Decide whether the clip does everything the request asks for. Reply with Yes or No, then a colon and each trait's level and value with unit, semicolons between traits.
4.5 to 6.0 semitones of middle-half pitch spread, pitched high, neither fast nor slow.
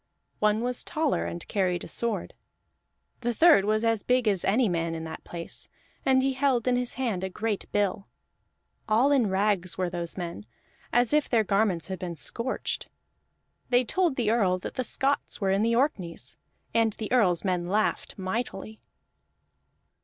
Yes: average, 5.0 semitones; high, 215 Hz; average, 170 wpm